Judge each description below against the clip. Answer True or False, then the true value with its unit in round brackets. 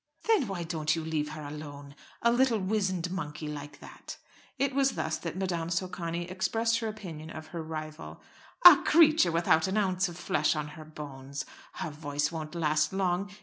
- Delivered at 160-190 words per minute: True (180 wpm)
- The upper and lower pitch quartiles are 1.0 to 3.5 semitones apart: False (4.0 semitones)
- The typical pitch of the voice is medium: True (170 Hz)